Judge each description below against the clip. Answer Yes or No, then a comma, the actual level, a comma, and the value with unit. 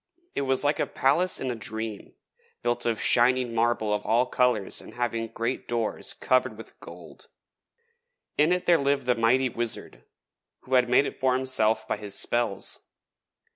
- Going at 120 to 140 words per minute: No, average, 170 wpm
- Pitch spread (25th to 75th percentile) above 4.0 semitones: No, narrow, 2.5 semitones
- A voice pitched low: Yes, low, 120 Hz